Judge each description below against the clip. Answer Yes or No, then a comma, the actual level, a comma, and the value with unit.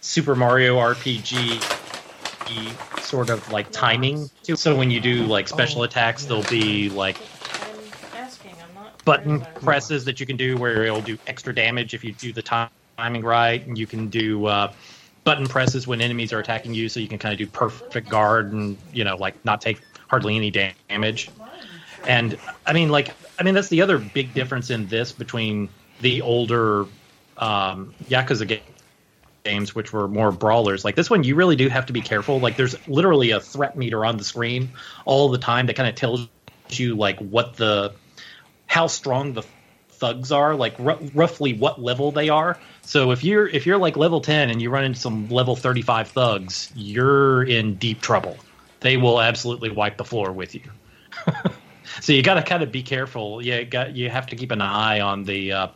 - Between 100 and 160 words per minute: No, average, 190 wpm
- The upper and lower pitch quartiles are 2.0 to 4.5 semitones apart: Yes, average, 3.8 semitones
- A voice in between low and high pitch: No, low, 120 Hz